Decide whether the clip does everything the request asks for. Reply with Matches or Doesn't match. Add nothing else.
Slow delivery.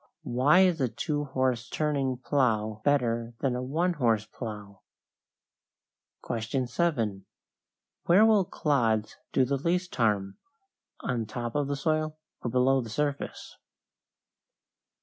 Matches